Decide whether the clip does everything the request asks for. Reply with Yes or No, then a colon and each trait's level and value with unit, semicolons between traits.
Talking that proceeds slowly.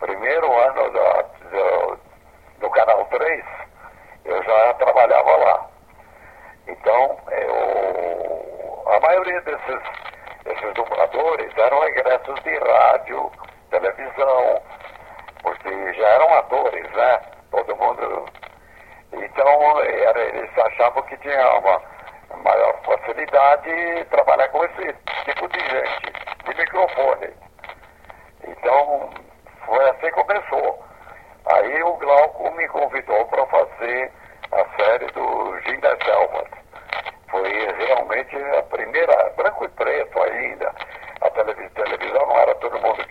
Yes: slow, 115 wpm